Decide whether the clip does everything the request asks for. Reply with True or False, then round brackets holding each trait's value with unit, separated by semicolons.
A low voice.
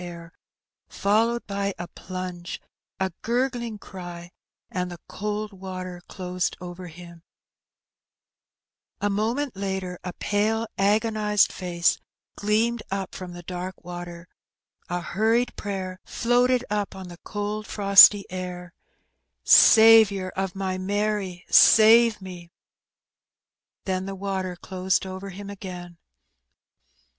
False (190 Hz)